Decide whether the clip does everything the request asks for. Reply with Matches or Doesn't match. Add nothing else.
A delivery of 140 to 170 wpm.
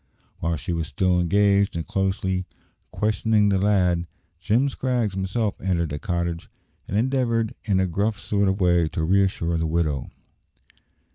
Matches